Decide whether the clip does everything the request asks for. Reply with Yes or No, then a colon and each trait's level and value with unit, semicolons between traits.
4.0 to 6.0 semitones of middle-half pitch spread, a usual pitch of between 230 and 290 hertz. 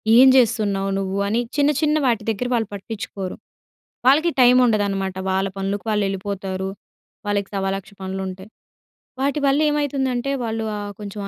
No: average, 4.3 semitones; high, 205 Hz